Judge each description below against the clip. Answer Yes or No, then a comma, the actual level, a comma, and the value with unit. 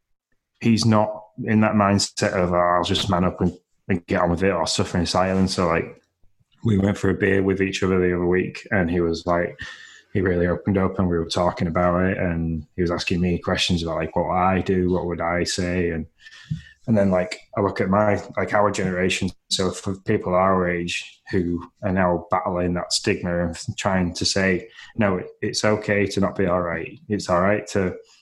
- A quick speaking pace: Yes, fast, 210 wpm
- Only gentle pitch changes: Yes, narrow, 2.2 semitones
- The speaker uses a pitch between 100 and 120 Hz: No, very low, 90 Hz